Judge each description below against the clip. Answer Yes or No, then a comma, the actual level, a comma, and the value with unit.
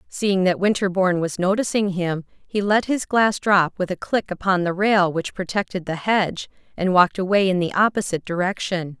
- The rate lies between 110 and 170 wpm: No, average, 185 wpm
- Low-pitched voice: No, high, 190 Hz